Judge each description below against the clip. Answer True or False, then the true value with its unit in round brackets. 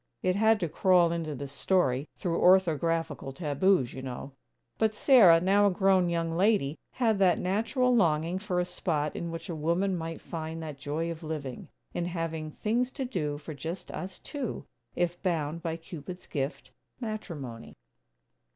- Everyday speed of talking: True (165 wpm)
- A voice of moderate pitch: True (170 Hz)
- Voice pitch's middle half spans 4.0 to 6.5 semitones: False (3.5 semitones)